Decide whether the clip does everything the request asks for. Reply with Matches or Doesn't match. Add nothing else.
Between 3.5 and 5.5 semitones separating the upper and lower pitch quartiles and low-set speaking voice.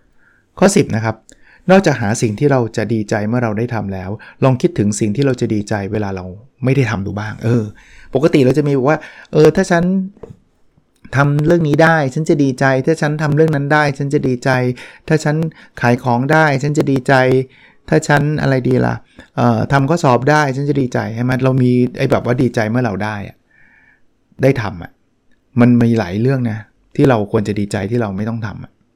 Matches